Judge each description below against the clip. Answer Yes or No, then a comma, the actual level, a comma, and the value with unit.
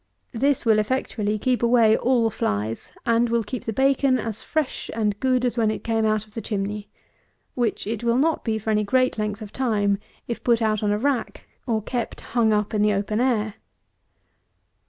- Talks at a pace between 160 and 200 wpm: Yes, average, 195 wpm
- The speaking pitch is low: No, high, 225 Hz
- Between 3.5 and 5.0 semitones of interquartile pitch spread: No, narrow, 2.5 semitones